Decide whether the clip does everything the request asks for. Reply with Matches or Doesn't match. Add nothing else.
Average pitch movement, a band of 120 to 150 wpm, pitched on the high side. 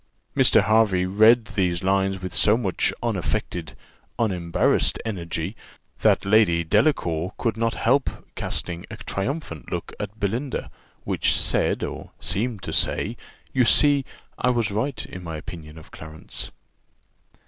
Doesn't match